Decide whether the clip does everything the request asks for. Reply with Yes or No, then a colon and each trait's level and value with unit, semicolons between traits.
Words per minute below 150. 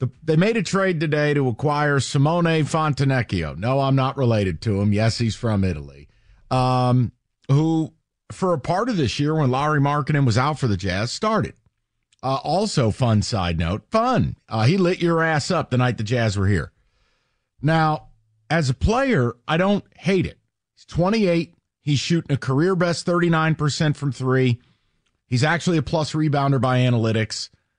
No: average, 170 wpm